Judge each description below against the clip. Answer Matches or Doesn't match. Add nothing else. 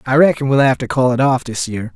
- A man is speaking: Matches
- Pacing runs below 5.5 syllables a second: Doesn't match